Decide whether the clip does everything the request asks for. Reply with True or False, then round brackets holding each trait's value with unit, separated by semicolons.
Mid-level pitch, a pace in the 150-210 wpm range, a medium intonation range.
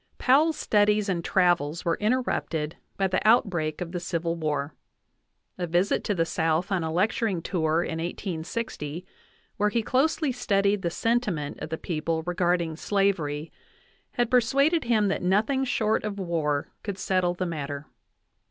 True (180 Hz; 155 wpm; 4.6 semitones)